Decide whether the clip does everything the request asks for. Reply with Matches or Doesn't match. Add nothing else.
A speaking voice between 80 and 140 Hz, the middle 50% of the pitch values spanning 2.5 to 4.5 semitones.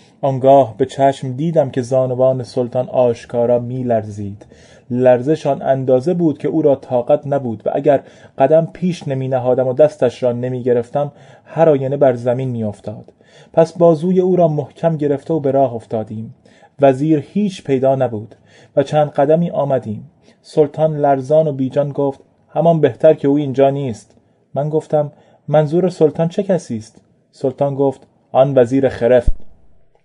Matches